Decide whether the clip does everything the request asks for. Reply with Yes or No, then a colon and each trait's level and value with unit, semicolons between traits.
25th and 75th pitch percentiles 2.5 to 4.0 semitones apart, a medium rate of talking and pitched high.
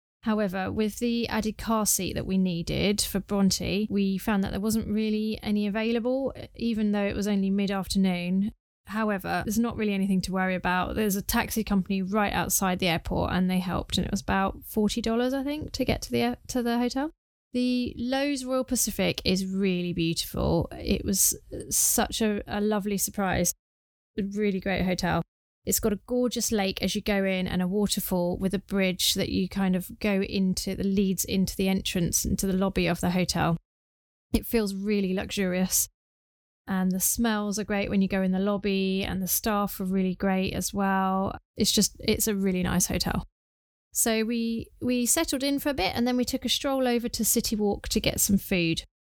Yes: average, 2.8 semitones; average, 195 wpm; high, 200 Hz